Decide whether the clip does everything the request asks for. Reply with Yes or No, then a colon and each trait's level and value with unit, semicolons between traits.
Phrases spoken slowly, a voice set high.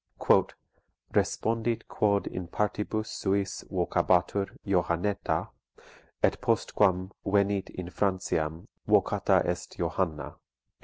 No: slow, 85 wpm; very low, 95 Hz